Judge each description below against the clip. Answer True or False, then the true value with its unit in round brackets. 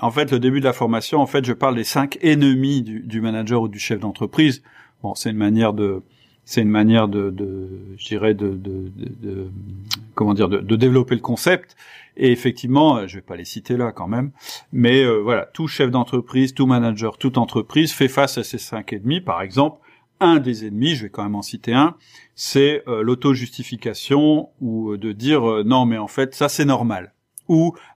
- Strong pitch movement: False (4.0 semitones)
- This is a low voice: True (120 Hz)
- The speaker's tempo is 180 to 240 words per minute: True (210 wpm)